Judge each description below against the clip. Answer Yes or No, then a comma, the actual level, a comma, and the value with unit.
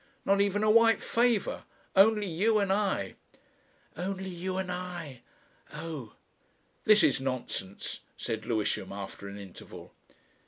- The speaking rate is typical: No, slow, 125 wpm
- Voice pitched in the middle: Yes, medium, 180 Hz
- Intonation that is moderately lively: No, wide, 8.2 semitones